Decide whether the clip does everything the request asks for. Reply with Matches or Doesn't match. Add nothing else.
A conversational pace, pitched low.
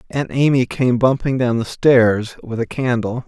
Matches